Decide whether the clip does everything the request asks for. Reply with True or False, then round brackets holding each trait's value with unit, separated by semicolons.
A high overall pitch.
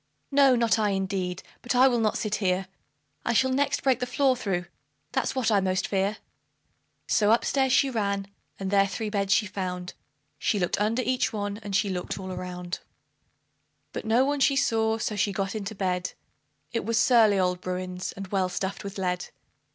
True (205 Hz)